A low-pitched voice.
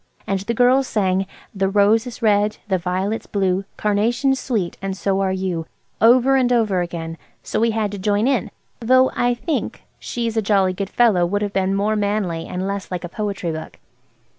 No: high, 205 Hz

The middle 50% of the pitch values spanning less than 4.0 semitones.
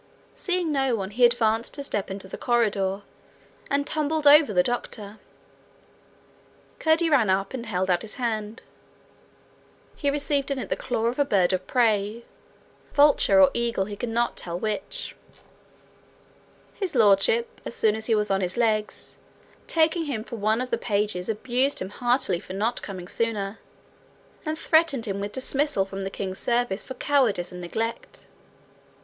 No: average, 5.3 semitones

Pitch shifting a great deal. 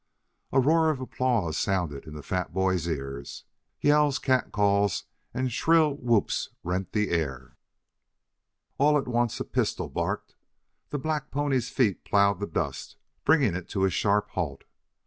Yes: wide, 7.1 semitones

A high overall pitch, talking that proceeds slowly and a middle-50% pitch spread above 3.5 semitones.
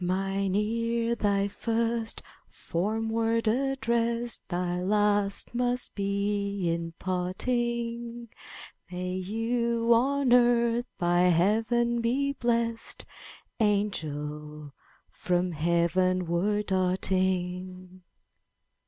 Yes: high, 205 Hz; slow, 80 wpm; average, 4.2 semitones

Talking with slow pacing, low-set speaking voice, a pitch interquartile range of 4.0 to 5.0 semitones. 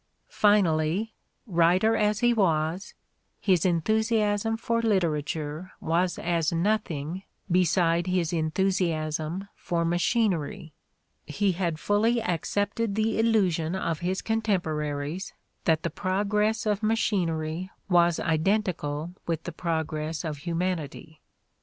No: slow, 105 wpm; medium, 175 Hz; average, 4.4 semitones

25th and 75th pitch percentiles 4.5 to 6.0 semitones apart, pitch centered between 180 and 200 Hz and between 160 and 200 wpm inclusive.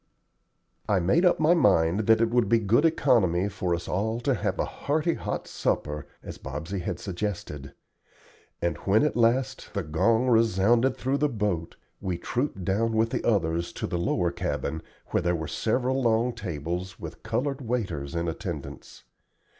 No: wide, 5.6 semitones; low, 105 Hz; average, 170 wpm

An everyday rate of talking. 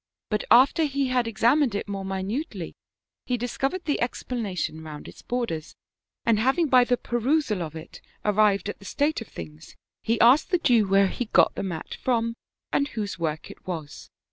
Yes: average, 185 wpm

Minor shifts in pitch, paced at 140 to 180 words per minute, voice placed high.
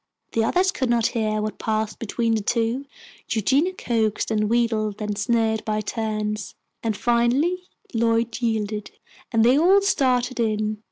Yes: narrow, 2.2 semitones; average, 150 wpm; high, 225 Hz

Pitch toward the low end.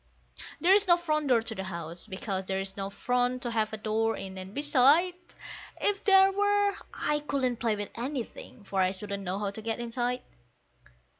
No: high, 230 Hz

